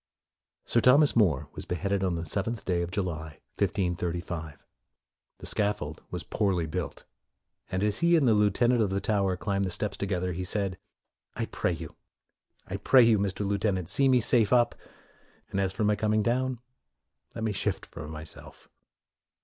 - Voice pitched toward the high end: No, low, 100 Hz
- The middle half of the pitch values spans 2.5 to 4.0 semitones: Yes, average, 3.4 semitones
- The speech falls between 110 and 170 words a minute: No, average, 180 wpm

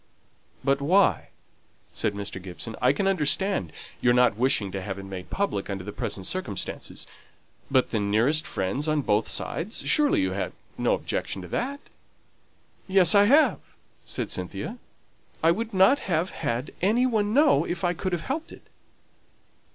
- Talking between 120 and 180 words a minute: Yes, average, 165 wpm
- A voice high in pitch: No, medium, 155 Hz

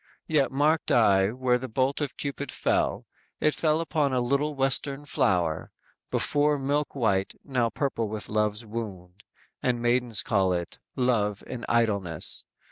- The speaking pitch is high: No, low, 125 Hz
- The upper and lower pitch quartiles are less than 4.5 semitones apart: No, average, 4.9 semitones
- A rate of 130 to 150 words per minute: Yes, average, 145 wpm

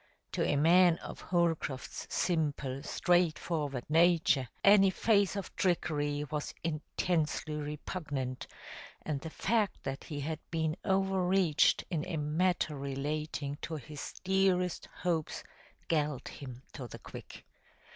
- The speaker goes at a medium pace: No, slow, 120 wpm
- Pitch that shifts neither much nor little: Yes, average, 3.6 semitones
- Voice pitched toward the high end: No, medium, 155 Hz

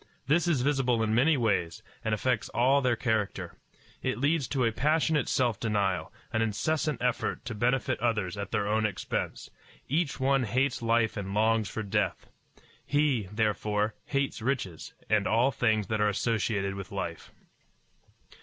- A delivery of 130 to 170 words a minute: Yes, average, 155 wpm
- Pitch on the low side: Yes, low, 115 Hz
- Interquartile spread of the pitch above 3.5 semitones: Yes, average, 4.0 semitones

